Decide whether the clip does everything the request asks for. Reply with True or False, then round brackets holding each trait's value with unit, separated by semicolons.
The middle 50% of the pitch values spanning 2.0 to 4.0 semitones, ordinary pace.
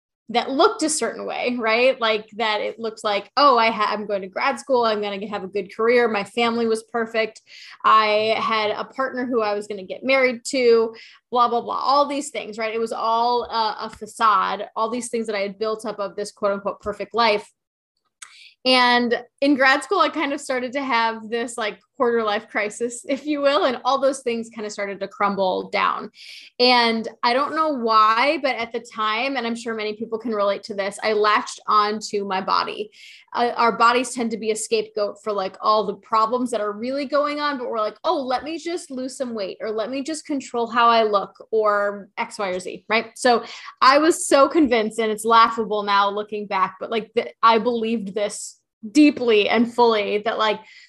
False (3.2 semitones; 215 wpm)